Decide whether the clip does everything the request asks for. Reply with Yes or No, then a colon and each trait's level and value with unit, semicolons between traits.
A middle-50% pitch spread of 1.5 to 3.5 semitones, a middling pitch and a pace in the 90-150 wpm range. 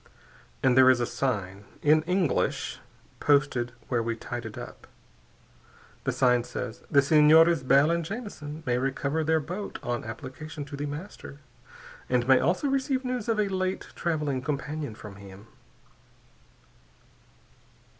No: average, 4.8 semitones; medium, 145 Hz; average, 140 wpm